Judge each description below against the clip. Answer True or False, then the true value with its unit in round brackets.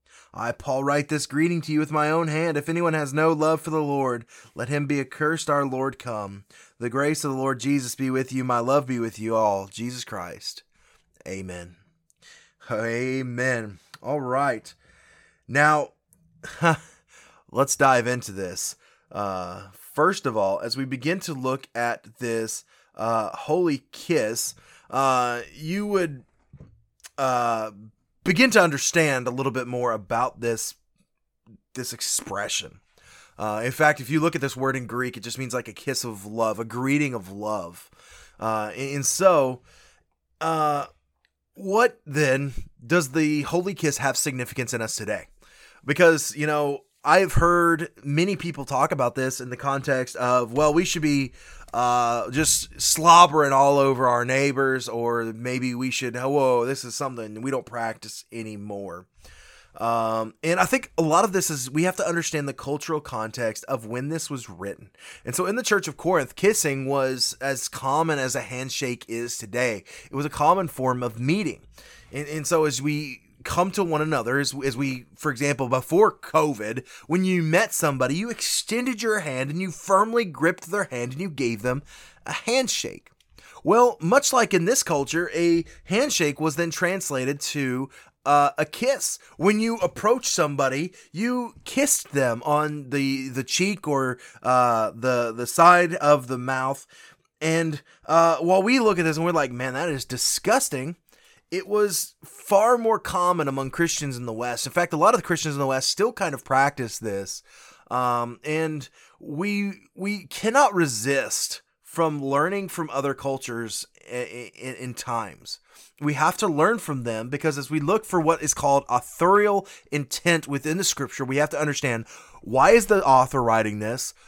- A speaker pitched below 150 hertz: True (140 Hz)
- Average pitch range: True (5.0 semitones)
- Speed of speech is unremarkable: True (170 wpm)